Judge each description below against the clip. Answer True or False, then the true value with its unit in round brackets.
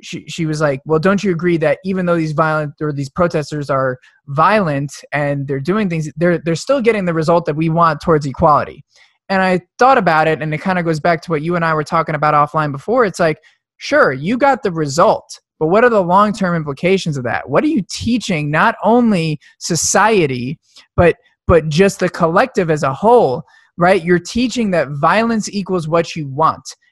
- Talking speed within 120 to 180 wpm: False (205 wpm)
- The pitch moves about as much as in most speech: True (4.1 semitones)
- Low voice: False (170 Hz)